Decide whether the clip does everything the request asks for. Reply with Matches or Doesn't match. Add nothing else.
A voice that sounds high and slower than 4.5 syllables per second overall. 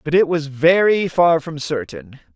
Doesn't match